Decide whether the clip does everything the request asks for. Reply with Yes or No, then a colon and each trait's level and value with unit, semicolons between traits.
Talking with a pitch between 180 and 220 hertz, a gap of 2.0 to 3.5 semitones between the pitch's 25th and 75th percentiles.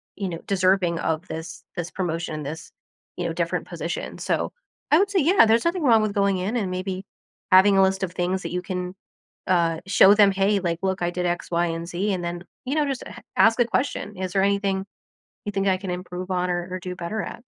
Yes: high, 190 Hz; narrow, 2.4 semitones